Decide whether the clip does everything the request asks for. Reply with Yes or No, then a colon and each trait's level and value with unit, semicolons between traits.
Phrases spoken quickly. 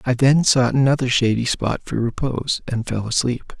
No: average, 185 wpm